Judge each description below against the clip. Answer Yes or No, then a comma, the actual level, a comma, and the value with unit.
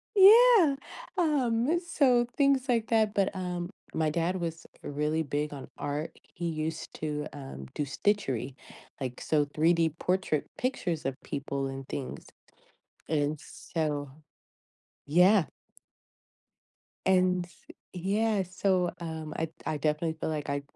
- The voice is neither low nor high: Yes, medium, 165 Hz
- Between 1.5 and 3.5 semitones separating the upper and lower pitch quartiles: No, wide, 5.6 semitones